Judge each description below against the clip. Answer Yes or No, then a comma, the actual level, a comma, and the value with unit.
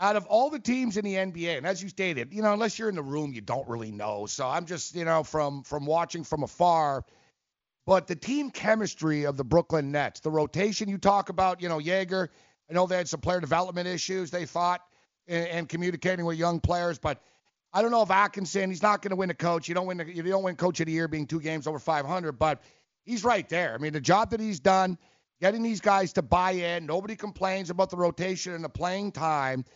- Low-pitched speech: No, medium, 175 Hz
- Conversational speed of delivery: No, fast, 240 wpm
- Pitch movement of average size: Yes, average, 3.2 semitones